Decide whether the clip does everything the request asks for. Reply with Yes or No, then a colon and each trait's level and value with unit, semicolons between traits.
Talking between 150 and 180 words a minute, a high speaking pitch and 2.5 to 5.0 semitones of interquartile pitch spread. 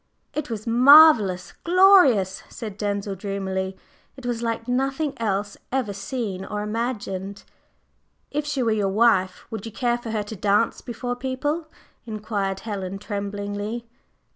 No: average, 140 wpm; high, 215 Hz; average, 3.7 semitones